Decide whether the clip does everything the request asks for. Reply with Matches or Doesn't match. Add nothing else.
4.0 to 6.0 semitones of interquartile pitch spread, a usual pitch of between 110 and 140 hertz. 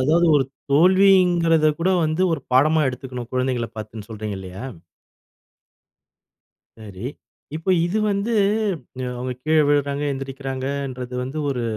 Matches